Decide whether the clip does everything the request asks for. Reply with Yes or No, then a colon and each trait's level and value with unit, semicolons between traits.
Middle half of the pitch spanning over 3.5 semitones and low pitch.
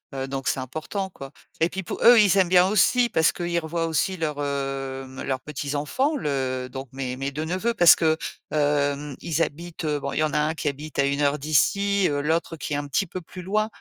No: average, 4.1 semitones; medium, 150 Hz